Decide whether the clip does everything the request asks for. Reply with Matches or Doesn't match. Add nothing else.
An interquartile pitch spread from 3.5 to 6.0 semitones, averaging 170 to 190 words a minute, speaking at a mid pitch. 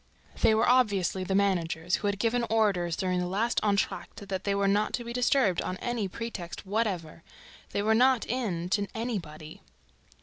Doesn't match